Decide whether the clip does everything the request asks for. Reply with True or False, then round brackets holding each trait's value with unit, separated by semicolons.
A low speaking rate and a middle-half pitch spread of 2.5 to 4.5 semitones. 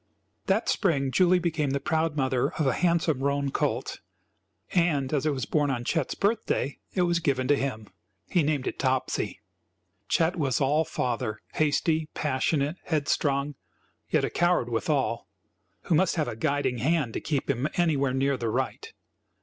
False (165 wpm; 3.5 semitones)